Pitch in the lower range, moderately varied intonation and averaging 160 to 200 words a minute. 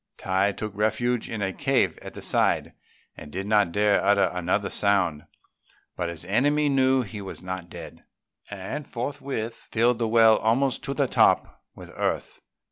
Yes: low, 105 Hz; average, 4.2 semitones; average, 170 wpm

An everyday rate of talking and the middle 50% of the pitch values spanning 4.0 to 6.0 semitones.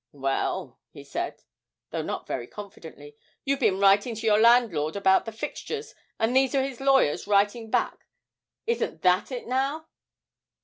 Yes: average, 150 wpm; wide, 5.4 semitones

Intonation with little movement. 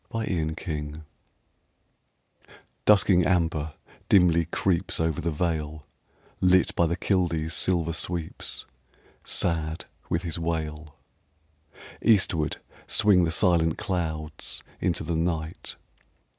Yes: narrow, 2.3 semitones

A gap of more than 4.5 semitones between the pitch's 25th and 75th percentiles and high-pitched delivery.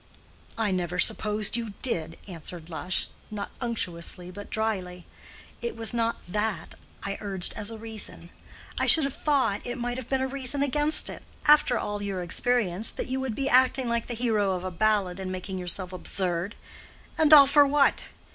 Yes: average, 5.2 semitones; high, 215 Hz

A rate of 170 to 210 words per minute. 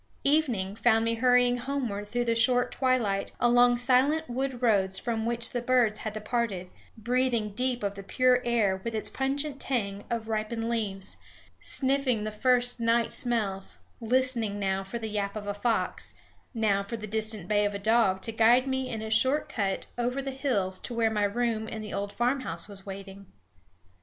Yes: average, 180 wpm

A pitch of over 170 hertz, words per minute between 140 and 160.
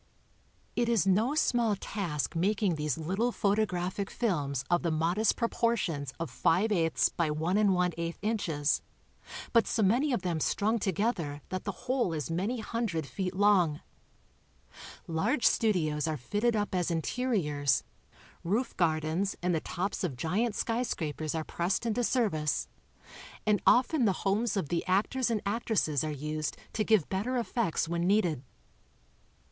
Yes: high, 190 Hz; average, 150 wpm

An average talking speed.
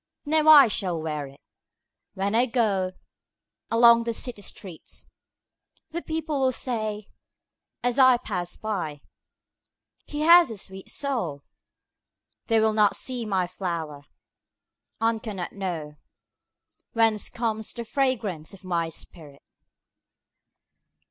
No: slow, 95 wpm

